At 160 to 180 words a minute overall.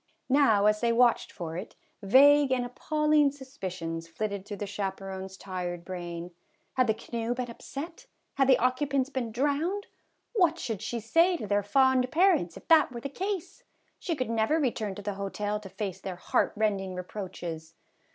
Yes: average, 170 wpm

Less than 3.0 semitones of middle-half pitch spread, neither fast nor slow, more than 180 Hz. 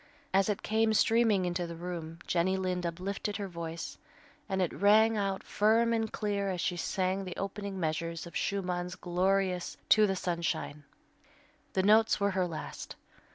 Yes: narrow, 2.5 semitones; average, 160 wpm; high, 190 Hz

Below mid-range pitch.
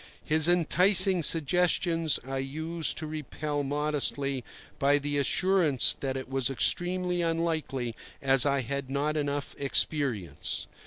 No: medium, 145 Hz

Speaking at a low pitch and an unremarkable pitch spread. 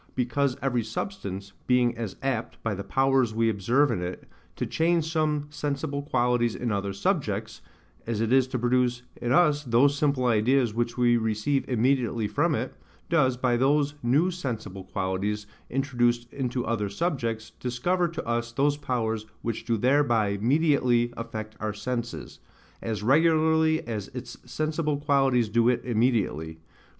Yes: low, 120 Hz; average, 3.9 semitones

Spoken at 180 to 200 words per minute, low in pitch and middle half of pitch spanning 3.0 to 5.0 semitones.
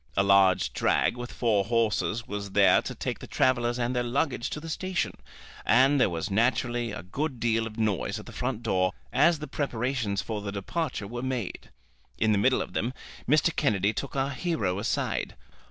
Yes: average, 190 wpm; low, 120 Hz; average, 4.2 semitones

